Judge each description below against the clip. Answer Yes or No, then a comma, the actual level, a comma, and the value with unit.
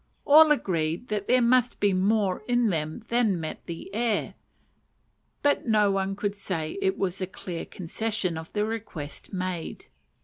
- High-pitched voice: Yes, high, 200 Hz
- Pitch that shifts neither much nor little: Yes, average, 4.0 semitones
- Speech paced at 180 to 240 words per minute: No, average, 160 wpm